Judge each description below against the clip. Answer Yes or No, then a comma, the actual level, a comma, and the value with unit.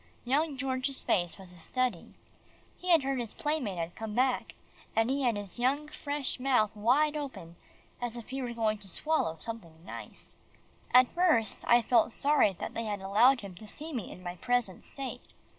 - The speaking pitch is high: Yes, high, 240 Hz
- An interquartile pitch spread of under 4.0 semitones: No, average, 4.9 semitones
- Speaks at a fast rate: No, average, 190 wpm